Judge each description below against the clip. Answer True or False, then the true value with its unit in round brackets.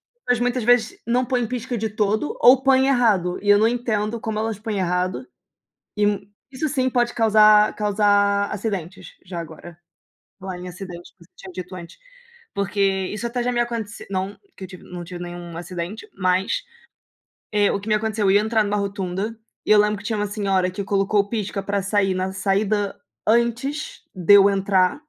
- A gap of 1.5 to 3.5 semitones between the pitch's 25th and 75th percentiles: True (3.0 semitones)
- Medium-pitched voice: False (205 Hz)